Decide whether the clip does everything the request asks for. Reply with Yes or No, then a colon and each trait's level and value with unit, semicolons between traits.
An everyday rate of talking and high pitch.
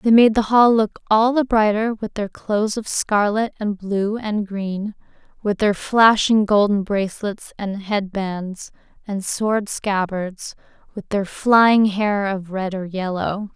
Yes: average, 160 wpm; high, 205 Hz